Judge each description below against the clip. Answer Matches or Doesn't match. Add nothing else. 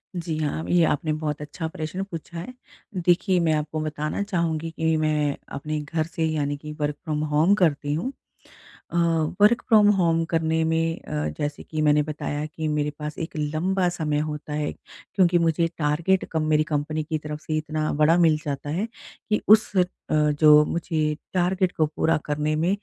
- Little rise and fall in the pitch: Matches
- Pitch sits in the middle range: Matches